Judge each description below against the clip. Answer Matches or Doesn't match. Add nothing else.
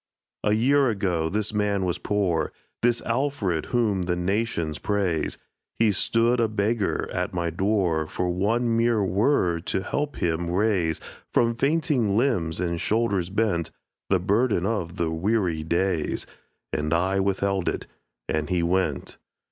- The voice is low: Matches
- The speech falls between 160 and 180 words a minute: Doesn't match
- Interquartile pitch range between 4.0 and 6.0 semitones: Matches